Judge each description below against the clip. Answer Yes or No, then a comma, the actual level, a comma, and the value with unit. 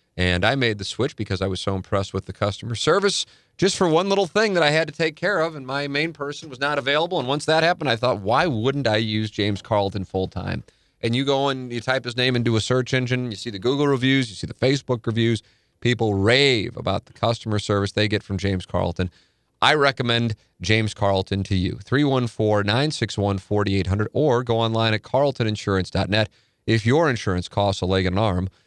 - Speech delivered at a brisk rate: Yes, fast, 215 wpm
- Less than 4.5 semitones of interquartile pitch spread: No, average, 5.2 semitones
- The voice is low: Yes, low, 115 Hz